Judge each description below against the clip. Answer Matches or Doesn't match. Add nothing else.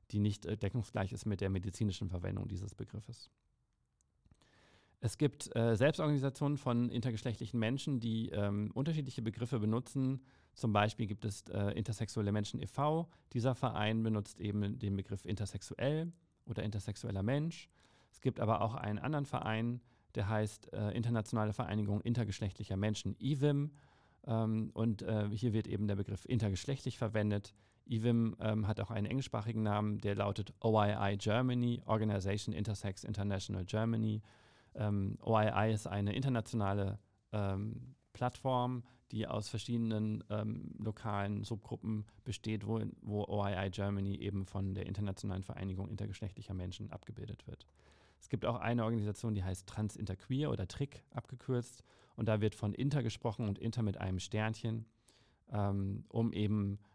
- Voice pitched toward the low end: Matches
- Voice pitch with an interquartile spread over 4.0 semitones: Doesn't match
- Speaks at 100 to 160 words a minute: Matches